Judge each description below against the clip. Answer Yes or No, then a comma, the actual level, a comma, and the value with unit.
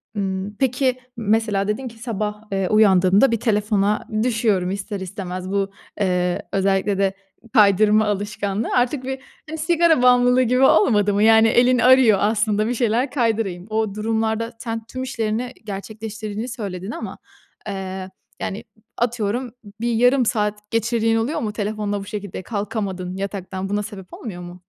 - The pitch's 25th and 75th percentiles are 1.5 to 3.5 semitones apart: Yes, average, 2.9 semitones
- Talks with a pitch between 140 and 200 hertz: No, high, 215 Hz